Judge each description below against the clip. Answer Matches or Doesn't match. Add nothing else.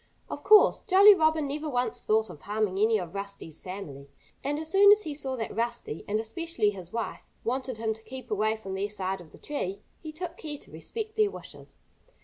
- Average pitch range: Doesn't match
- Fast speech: Matches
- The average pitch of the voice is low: Doesn't match